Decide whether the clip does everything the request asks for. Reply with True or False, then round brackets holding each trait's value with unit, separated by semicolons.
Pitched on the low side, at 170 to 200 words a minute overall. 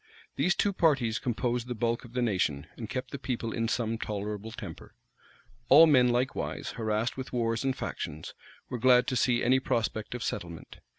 True (120 Hz; 180 wpm)